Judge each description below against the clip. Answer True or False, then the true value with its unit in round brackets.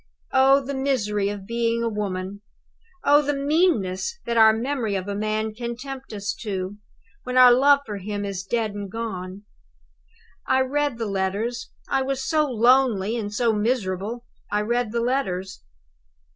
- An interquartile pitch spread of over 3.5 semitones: True (4.4 semitones)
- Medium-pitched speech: False (230 Hz)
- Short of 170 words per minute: True (160 wpm)